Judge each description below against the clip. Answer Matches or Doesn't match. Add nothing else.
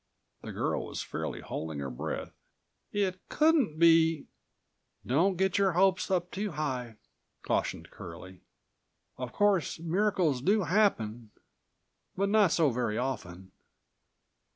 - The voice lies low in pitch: Doesn't match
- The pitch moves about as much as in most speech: Doesn't match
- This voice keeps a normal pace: Doesn't match